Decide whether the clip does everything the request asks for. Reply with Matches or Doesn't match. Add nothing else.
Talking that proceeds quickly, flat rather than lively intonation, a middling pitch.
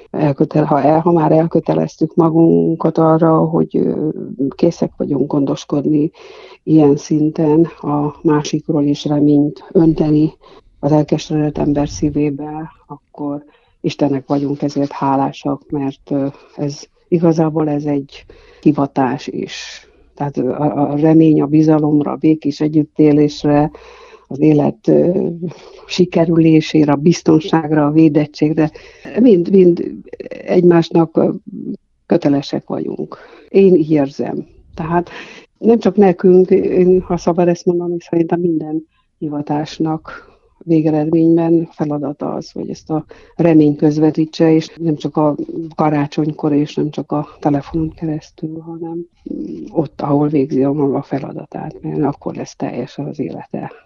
Doesn't match